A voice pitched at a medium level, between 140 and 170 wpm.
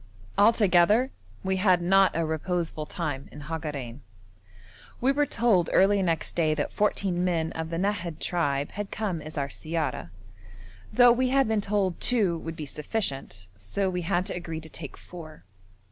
Yes: medium, 175 Hz; average, 165 wpm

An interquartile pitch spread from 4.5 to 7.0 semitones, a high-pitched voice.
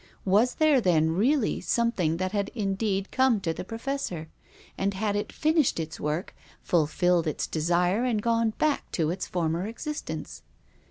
Yes: average, 5.3 semitones; high, 195 Hz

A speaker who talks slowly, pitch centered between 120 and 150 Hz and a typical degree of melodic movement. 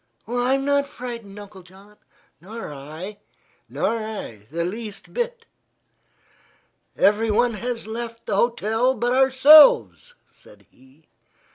No: slow, 110 wpm; high, 225 Hz; average, 4.0 semitones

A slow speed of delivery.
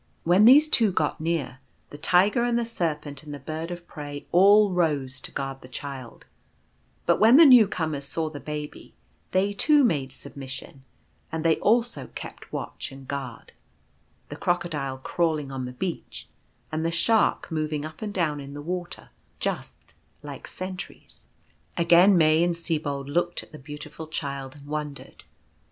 No: average, 170 wpm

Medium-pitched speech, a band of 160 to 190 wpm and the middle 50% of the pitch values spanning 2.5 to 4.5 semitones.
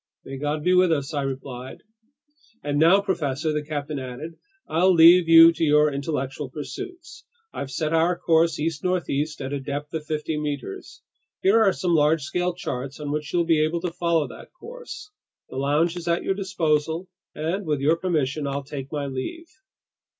Yes: medium, 155 Hz; average, 180 wpm; average, 3.2 semitones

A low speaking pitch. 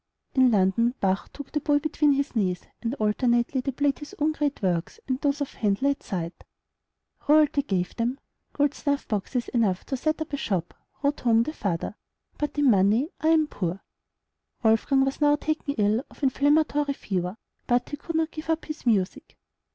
No: very high, 270 Hz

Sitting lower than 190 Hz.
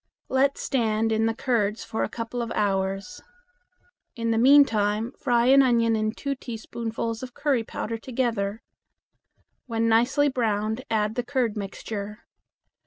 No: high, 230 Hz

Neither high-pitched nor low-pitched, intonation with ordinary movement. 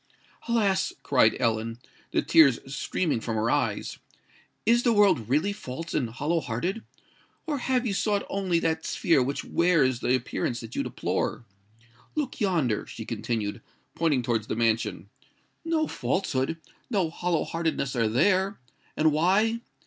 No: medium, 160 Hz; wide, 8.3 semitones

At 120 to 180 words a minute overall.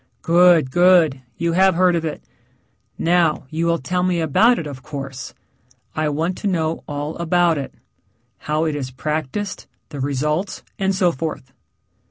Yes: average, 160 wpm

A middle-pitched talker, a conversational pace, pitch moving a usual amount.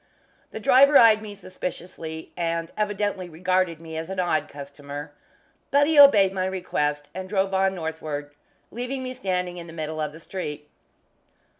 Yes: medium, 180 Hz; average, 160 wpm; average, 4.2 semitones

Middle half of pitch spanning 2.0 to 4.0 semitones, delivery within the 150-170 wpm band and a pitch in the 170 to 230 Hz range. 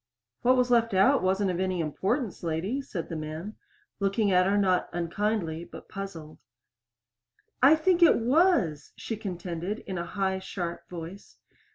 No: average, 4.6 semitones; average, 155 wpm; high, 190 Hz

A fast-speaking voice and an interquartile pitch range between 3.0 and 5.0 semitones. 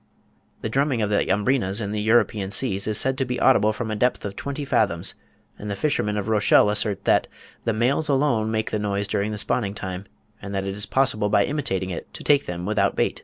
Yes: fast, 225 wpm; average, 3.7 semitones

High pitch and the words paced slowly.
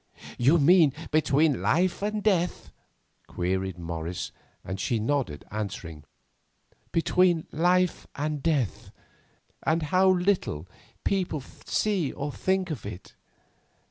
No: medium, 150 Hz; slow, 110 wpm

